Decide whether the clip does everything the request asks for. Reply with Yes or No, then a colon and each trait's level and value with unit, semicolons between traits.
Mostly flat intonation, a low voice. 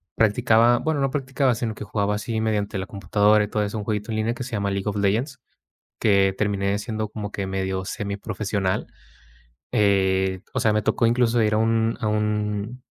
Yes: narrow, 2.0 semitones; low, 105 Hz